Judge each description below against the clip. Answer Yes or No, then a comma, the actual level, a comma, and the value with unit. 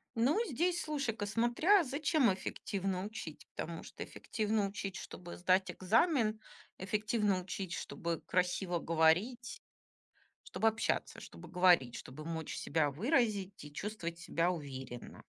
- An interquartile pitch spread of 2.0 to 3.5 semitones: No, average, 5.1 semitones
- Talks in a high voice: Yes, high, 195 Hz